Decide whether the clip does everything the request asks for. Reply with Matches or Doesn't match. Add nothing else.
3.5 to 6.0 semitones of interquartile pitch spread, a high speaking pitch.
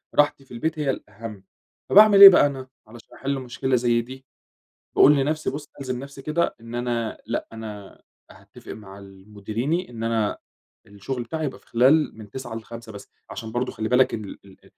Doesn't match